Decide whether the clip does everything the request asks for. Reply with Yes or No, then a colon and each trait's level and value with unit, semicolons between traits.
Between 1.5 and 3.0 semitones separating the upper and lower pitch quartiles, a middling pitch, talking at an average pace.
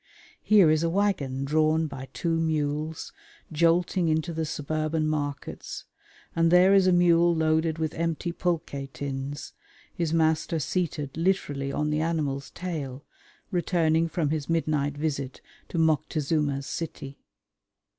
No: narrow, 2.4 semitones; medium, 155 Hz; slow, 130 wpm